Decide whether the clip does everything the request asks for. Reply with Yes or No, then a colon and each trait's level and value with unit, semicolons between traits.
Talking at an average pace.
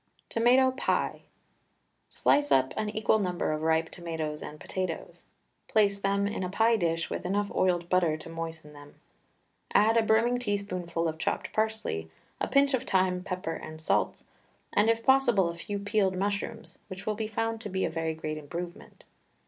Yes: average, 175 wpm